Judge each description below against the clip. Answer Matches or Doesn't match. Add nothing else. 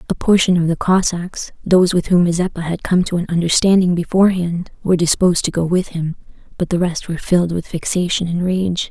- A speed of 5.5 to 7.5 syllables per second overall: Matches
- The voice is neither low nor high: Matches